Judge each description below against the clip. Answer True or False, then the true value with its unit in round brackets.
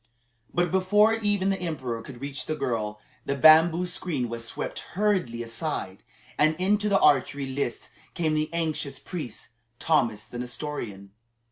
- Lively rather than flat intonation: True (6.8 semitones)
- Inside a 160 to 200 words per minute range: False (145 wpm)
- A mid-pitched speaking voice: True (155 Hz)